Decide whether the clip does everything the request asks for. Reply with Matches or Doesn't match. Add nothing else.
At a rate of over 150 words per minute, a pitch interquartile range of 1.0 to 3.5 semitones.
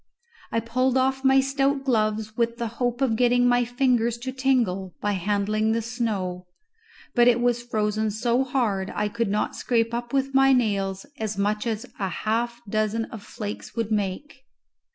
Matches